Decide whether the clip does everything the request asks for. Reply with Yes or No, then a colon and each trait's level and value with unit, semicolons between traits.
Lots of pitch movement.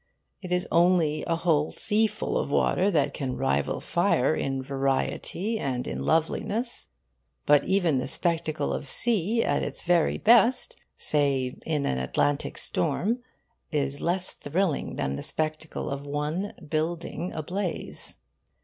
No: average, 4.7 semitones